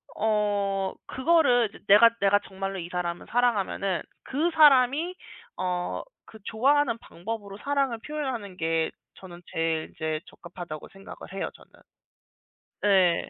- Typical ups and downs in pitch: No, wide, 5.7 semitones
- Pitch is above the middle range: Yes, high, 200 Hz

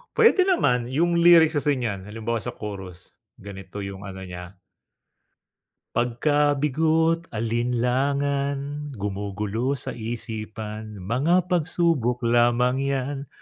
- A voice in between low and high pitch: No, low, 125 Hz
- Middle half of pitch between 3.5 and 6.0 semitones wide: Yes, wide, 5.4 semitones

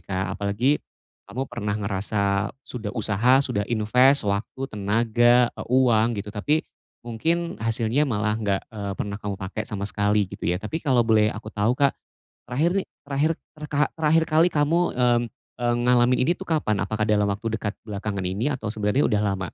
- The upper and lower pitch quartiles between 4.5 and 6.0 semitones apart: No, average, 4.1 semitones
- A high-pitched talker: No, low, 110 Hz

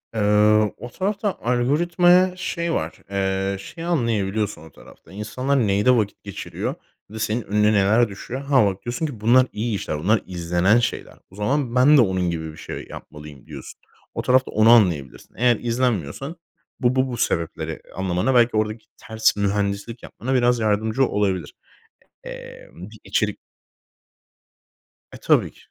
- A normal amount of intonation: Yes, average, 4.6 semitones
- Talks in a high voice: No, low, 110 Hz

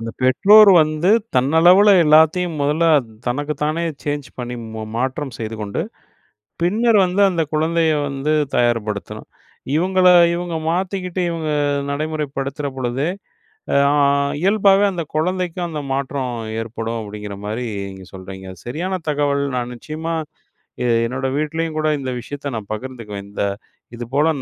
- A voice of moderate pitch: Yes, medium, 150 Hz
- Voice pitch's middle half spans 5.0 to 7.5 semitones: Yes, wide, 5.6 semitones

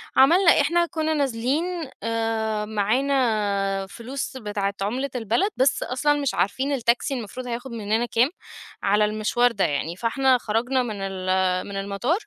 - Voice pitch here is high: Yes, high, 230 Hz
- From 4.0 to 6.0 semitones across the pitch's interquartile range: Yes, average, 4.5 semitones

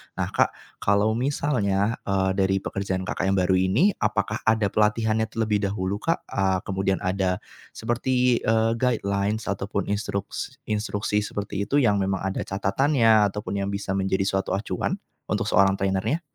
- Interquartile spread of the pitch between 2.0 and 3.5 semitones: Yes, narrow, 2.4 semitones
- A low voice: Yes, low, 100 Hz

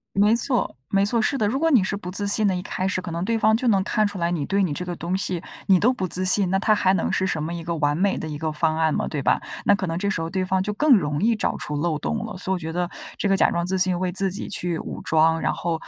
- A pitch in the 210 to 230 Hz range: No, medium, 185 Hz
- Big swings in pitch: No, average, 3.3 semitones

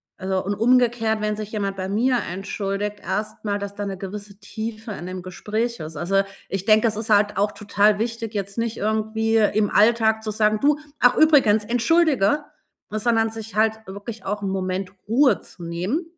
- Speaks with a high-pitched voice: Yes, high, 215 Hz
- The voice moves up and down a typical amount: No, narrow, 2.2 semitones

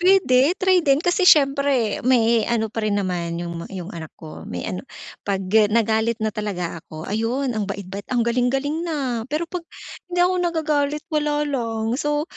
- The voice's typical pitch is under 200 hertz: No, high, 240 Hz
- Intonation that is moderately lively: No, wide, 6.0 semitones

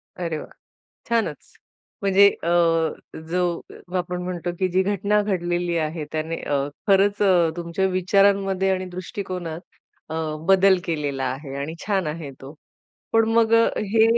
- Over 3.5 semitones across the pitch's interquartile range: No, average, 3.1 semitones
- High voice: No, medium, 180 Hz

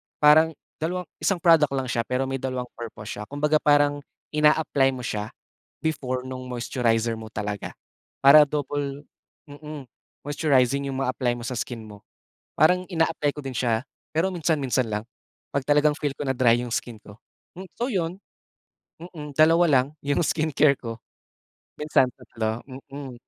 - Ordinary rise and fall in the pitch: Yes, average, 3.7 semitones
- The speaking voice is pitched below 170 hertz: Yes, medium, 140 Hz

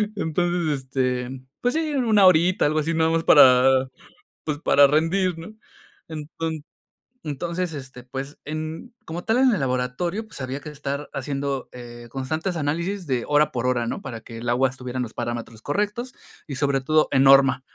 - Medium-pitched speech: Yes, medium, 145 Hz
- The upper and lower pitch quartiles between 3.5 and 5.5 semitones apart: Yes, average, 4.5 semitones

